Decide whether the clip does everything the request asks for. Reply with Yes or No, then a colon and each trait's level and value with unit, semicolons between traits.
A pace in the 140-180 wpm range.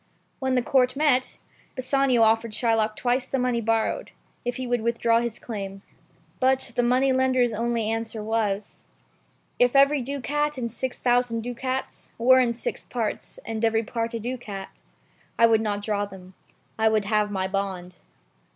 Yes: average, 165 wpm